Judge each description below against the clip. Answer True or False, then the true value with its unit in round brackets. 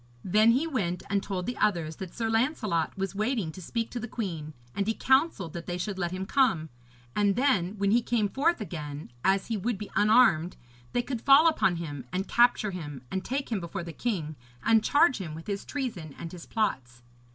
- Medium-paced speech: False (210 wpm)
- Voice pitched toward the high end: True (200 Hz)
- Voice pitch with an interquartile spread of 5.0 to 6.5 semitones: True (5.6 semitones)